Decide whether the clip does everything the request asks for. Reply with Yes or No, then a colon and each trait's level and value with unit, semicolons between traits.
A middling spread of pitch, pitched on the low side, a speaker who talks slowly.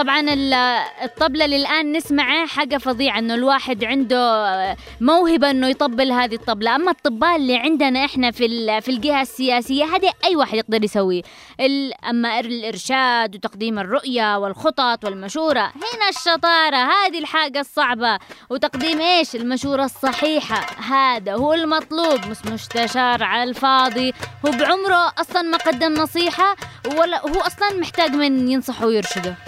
No: average, 4.9 semitones; very high, 270 Hz; slow, 130 wpm